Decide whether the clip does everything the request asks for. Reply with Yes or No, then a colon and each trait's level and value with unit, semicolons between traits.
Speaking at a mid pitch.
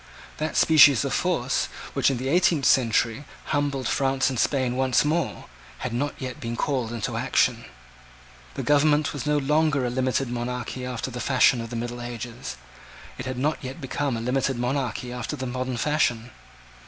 No: low, 130 Hz